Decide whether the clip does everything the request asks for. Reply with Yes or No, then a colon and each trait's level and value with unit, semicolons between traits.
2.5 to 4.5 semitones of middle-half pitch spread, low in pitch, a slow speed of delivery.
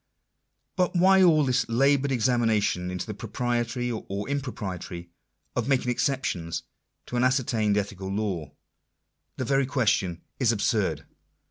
No: average, 5.1 semitones; low, 120 Hz; slow, 125 wpm